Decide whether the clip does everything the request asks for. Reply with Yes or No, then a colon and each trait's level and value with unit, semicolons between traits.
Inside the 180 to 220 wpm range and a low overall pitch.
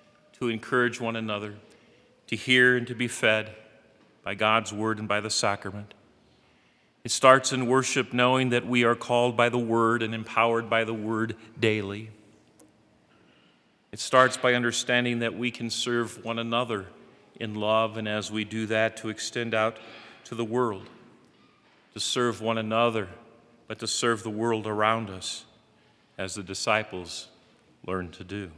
No: average, 155 wpm; low, 115 Hz